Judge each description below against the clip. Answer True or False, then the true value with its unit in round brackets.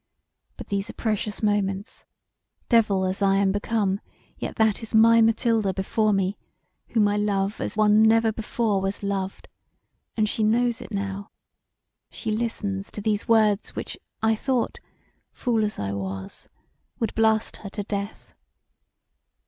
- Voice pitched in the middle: False (210 Hz)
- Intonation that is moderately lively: False (2.1 semitones)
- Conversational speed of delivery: True (150 wpm)